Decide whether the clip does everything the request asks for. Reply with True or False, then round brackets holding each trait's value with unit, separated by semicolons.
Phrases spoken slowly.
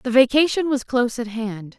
False (200 wpm)